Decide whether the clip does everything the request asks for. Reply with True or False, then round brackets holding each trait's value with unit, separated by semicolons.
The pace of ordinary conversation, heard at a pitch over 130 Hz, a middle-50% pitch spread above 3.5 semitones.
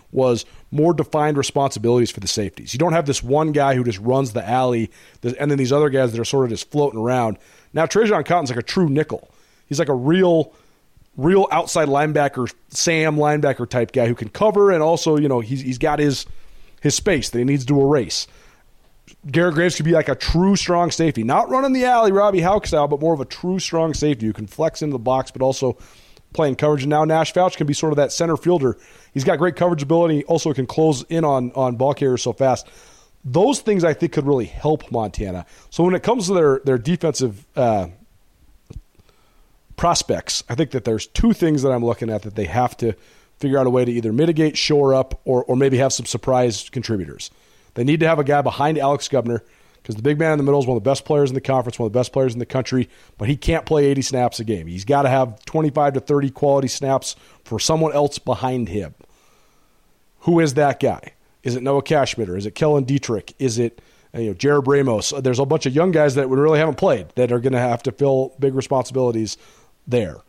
False (230 wpm; 140 Hz; 4.2 semitones)